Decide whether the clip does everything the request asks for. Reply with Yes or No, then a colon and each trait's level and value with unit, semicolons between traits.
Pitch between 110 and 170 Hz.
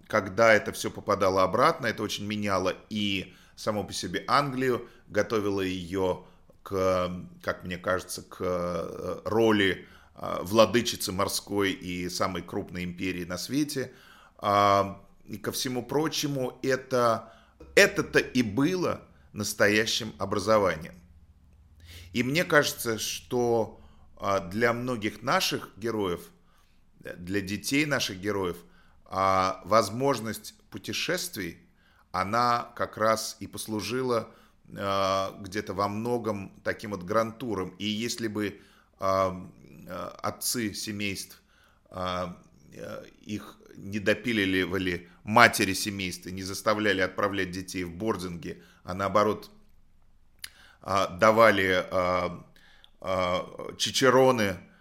No: low, 100 Hz